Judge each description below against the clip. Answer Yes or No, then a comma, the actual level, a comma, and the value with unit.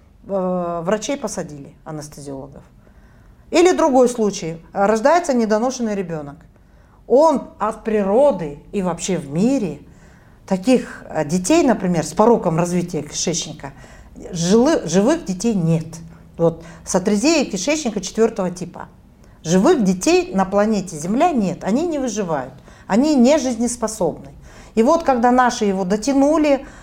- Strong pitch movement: Yes, wide, 6.7 semitones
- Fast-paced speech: No, slow, 110 wpm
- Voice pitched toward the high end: Yes, high, 195 Hz